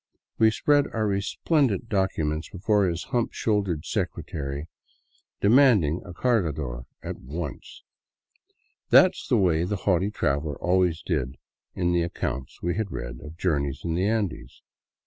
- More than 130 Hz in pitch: No, very low, 90 Hz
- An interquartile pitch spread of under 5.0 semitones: No, average, 5.3 semitones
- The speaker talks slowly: No, average, 145 wpm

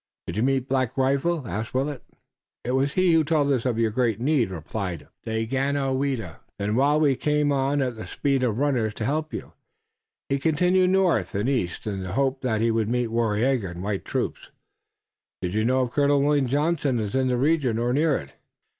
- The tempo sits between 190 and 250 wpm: Yes, average, 200 wpm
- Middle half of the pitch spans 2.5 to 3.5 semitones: No, average, 4.3 semitones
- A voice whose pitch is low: Yes, low, 130 Hz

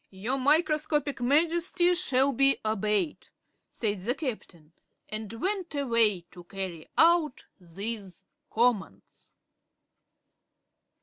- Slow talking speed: Yes, slow, 95 wpm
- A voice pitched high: Yes, high, 245 Hz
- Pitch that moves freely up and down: Yes, wide, 7.0 semitones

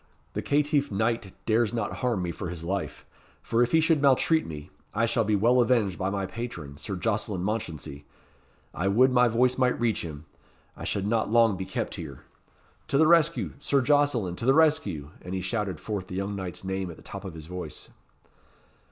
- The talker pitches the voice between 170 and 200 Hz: No, low, 105 Hz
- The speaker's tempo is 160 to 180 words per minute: No, average, 200 wpm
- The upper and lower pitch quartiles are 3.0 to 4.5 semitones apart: No, average, 5.1 semitones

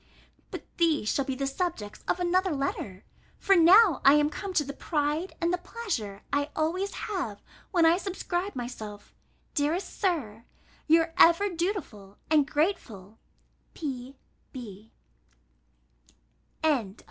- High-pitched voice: Yes, very high, 305 Hz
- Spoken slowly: Yes, slow, 125 wpm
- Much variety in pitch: Yes, wide, 6.1 semitones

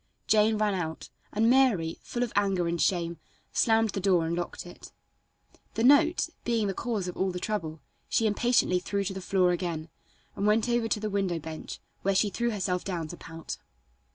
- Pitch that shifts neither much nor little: Yes, average, 4.0 semitones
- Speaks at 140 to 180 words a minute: No, average, 195 wpm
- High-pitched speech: Yes, high, 195 Hz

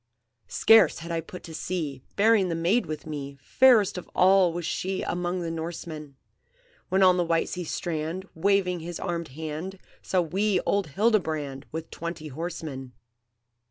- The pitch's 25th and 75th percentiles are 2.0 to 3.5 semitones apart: Yes, average, 3.1 semitones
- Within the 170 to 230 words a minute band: No, average, 160 wpm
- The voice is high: No, medium, 170 Hz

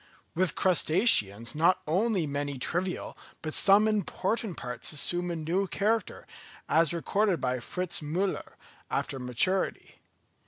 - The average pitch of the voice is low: No, medium, 175 Hz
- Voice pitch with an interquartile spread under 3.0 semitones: No, average, 4.5 semitones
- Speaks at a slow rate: Yes, slow, 120 wpm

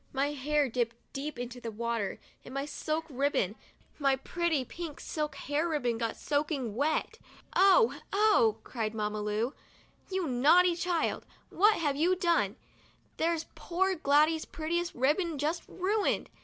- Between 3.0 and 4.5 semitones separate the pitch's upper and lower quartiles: No, wide, 5.4 semitones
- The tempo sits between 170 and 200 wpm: No, average, 155 wpm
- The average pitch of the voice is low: No, very high, 295 Hz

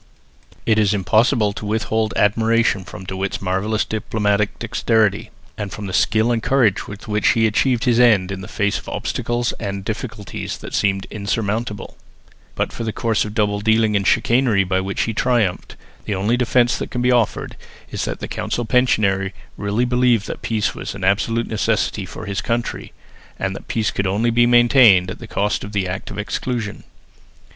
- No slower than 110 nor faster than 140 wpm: No, average, 185 wpm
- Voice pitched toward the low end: Yes, low, 110 Hz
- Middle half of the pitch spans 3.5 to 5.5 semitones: No, average, 2.7 semitones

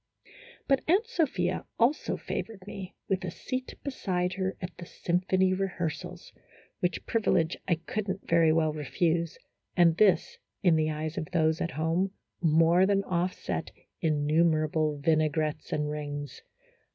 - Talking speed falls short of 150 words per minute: Yes, average, 140 wpm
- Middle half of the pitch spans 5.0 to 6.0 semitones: No, average, 3.1 semitones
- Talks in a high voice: No, medium, 175 Hz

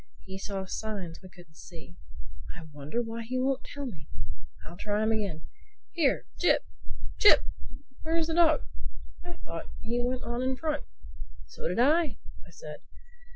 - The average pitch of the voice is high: Yes, high, 230 Hz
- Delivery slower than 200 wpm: Yes, average, 155 wpm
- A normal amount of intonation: No, wide, 7.2 semitones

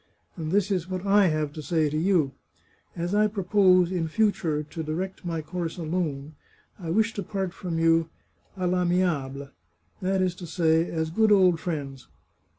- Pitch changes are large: No, average, 3.1 semitones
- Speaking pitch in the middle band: Yes, medium, 175 Hz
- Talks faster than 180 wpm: Yes, average, 190 wpm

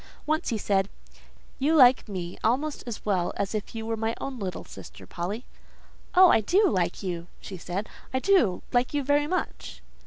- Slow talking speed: No, average, 175 wpm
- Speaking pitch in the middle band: No, high, 225 Hz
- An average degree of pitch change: No, wide, 6.9 semitones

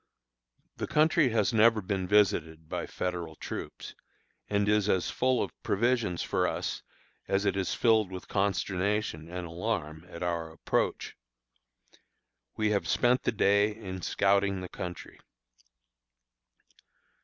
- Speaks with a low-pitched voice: Yes, low, 100 Hz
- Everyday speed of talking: No, slow, 130 wpm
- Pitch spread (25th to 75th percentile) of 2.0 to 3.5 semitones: Yes, average, 3.2 semitones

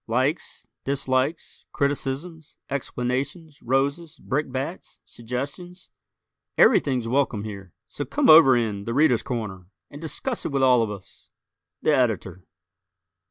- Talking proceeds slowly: Yes, slow, 115 wpm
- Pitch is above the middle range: No, low, 135 Hz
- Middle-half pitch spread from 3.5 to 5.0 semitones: Yes, average, 4.0 semitones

